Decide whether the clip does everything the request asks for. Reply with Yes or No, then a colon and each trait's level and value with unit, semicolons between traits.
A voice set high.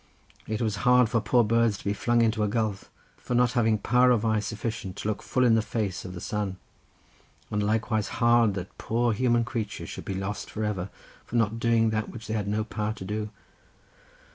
No: low, 110 Hz